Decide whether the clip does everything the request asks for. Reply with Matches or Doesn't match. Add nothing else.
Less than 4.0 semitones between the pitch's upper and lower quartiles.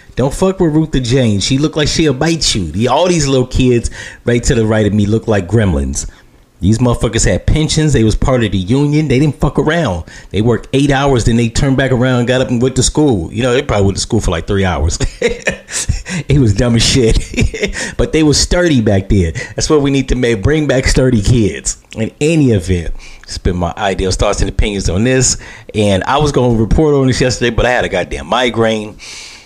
Doesn't match